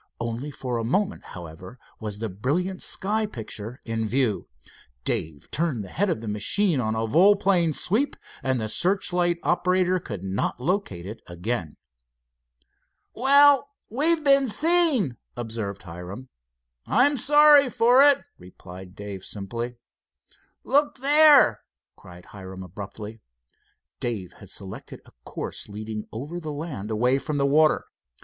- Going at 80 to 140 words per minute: Yes, slow, 135 wpm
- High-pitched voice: No, low, 130 Hz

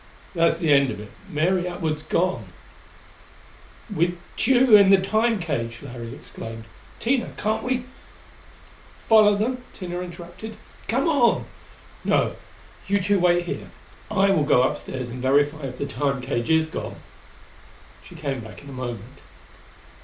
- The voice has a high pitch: No, medium, 170 Hz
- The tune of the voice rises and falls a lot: Yes, wide, 7.1 semitones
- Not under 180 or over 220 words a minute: No, average, 150 wpm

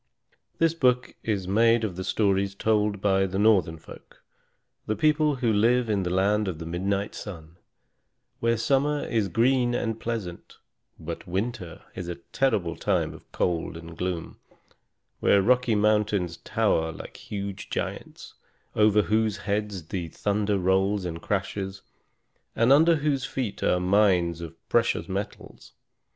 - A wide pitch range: No, average, 3.8 semitones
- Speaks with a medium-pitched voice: No, low, 100 Hz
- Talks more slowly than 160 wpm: Yes, average, 145 wpm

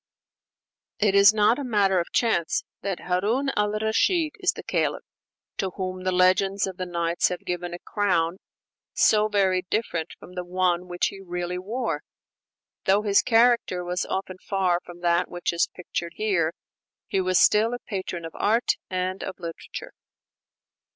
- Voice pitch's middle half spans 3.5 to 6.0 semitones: No, average, 2.9 semitones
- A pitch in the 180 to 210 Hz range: Yes, medium, 185 Hz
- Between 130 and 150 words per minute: No, average, 165 wpm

